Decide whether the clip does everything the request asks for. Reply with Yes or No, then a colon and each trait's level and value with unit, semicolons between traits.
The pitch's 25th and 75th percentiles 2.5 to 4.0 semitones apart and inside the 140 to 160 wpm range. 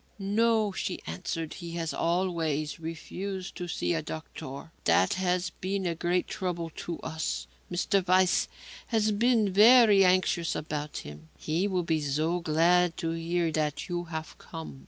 Yes: average, 2.8 semitones; average, 155 wpm